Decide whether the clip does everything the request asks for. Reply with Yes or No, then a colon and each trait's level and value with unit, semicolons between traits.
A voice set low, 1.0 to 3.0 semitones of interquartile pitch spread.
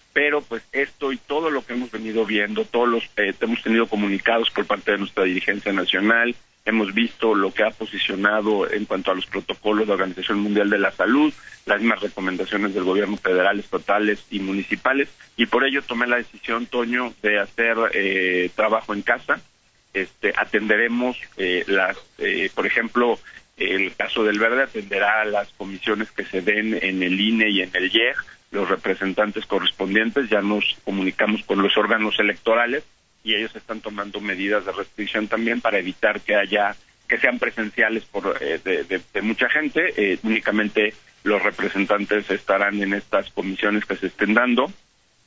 Yes: low, 110 Hz; narrow, 2.6 semitones